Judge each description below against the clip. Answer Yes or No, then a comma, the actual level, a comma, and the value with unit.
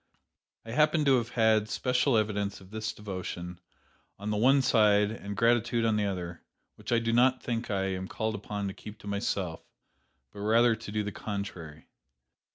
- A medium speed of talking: Yes, average, 180 wpm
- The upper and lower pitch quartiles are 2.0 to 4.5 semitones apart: Yes, narrow, 2.5 semitones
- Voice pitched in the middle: No, low, 105 Hz